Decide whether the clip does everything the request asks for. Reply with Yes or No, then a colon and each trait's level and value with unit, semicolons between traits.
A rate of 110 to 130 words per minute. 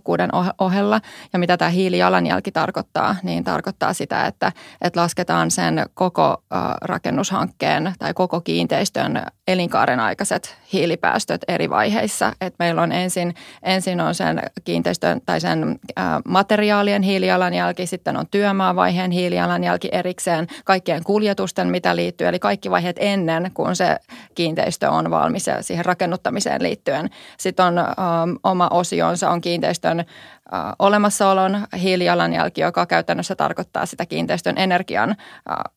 Yes: average, 115 wpm